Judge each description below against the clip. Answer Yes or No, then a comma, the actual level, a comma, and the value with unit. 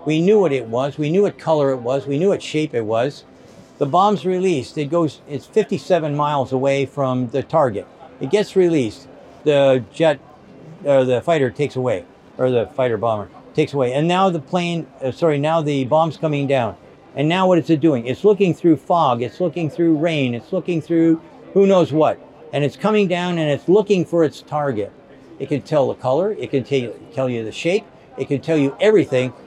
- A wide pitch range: No, average, 4.1 semitones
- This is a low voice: No, medium, 150 Hz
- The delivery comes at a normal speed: No, fast, 210 wpm